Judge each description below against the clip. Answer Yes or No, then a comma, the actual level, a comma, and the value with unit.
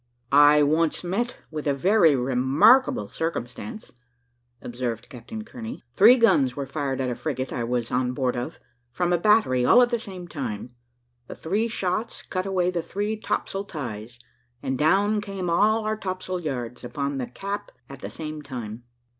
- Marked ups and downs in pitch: Yes, wide, 7.8 semitones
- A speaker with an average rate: Yes, average, 170 wpm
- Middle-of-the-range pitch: Yes, medium, 155 Hz